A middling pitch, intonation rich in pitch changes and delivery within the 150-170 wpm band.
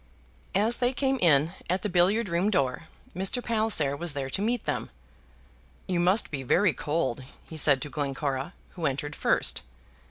Yes: medium, 170 Hz; wide, 6.5 semitones; average, 165 wpm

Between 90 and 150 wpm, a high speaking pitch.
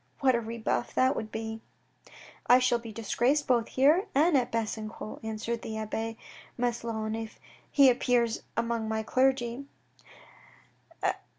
Yes: slow, 135 wpm; high, 235 Hz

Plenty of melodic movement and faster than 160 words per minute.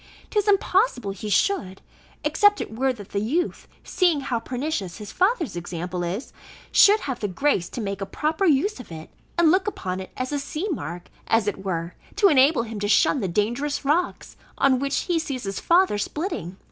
Yes: wide, 8.7 semitones; average, 195 wpm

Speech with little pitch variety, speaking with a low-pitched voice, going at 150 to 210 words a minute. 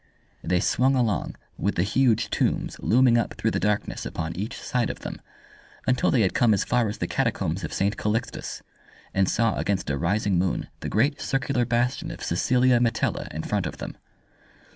No: average, 4.3 semitones; low, 110 Hz; average, 185 wpm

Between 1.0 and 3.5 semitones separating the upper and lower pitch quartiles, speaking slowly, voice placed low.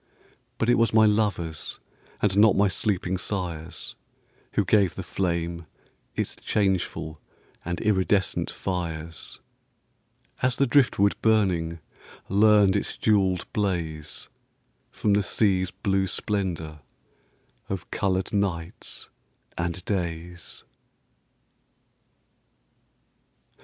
Yes: average, 3.2 semitones; slow, 95 wpm; very low, 95 Hz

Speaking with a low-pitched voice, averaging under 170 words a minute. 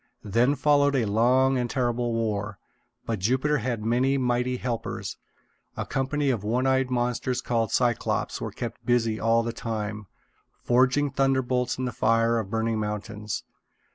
Yes: low, 120 Hz; average, 150 wpm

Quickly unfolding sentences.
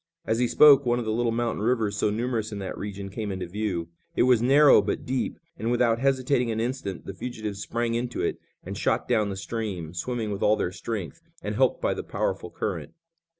Yes: fast, 215 wpm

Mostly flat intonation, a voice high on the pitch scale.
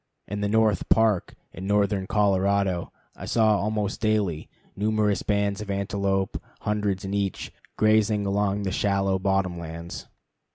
No: narrow, 1.3 semitones; low, 100 Hz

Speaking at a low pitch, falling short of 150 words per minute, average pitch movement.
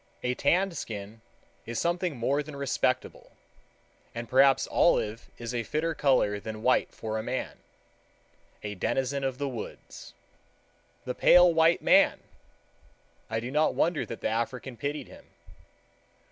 Yes: low, 130 Hz; slow, 135 wpm; average, 4.7 semitones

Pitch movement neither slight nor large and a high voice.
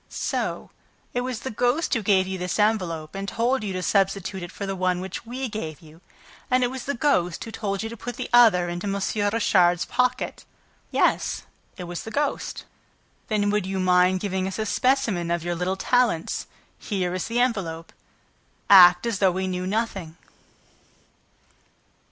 Yes: average, 4.2 semitones; high, 195 Hz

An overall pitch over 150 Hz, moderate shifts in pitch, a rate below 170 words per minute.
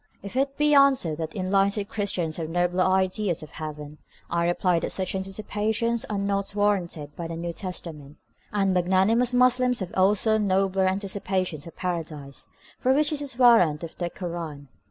No: high, 190 Hz; average, 3.7 semitones; average, 175 wpm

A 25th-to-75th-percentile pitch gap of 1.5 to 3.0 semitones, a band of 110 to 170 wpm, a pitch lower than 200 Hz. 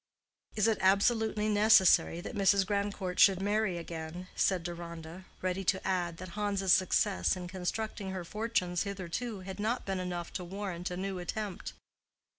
Yes: narrow, 2.5 semitones; average, 155 wpm; high, 190 Hz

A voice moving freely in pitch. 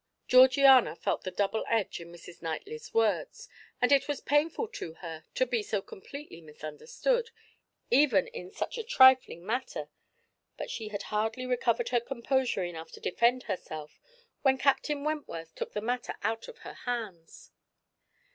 Yes: wide, 6.4 semitones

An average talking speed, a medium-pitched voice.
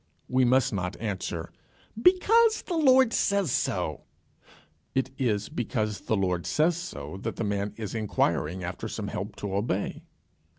No: average, 145 wpm; low, 110 Hz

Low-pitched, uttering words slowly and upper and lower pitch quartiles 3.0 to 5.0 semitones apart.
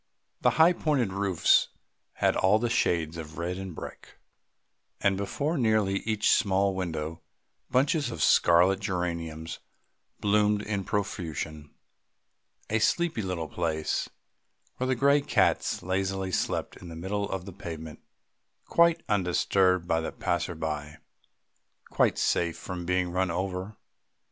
Yes: very low, 95 Hz; slow, 130 wpm; average, 3.7 semitones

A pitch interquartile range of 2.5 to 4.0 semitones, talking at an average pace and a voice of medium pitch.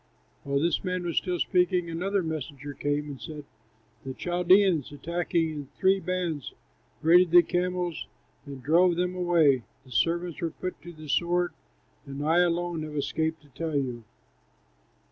Yes: average, 3.4 semitones; average, 155 wpm; medium, 165 Hz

